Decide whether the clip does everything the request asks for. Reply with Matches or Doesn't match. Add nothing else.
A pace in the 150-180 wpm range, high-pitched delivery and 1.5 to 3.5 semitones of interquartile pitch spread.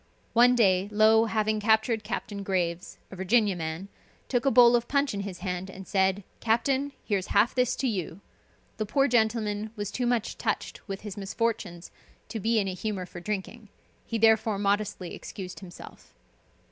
Matches